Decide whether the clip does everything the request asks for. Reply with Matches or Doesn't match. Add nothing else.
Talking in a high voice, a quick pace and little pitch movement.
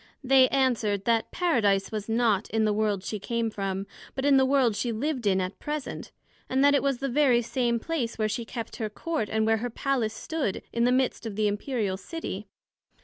Doesn't match